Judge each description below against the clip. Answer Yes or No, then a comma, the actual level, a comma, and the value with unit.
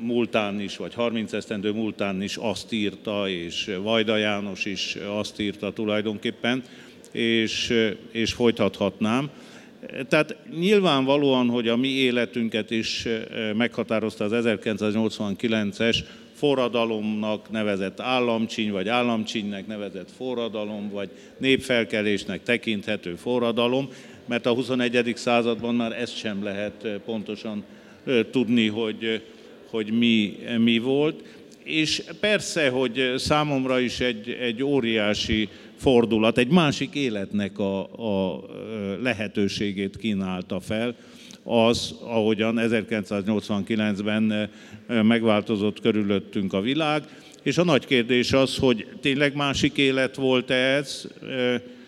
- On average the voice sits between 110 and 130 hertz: Yes, low, 115 Hz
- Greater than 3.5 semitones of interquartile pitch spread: No, average, 2.8 semitones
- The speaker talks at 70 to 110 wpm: Yes, slow, 105 wpm